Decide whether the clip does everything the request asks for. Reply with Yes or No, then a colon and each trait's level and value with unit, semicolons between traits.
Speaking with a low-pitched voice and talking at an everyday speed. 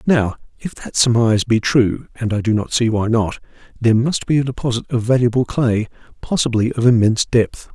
Yes: low, 115 Hz; average, 170 wpm